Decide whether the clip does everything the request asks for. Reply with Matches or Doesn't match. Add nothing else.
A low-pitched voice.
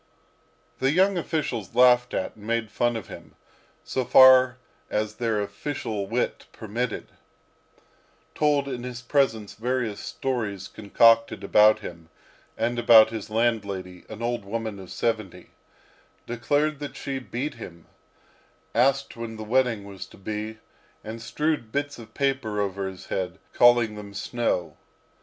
Matches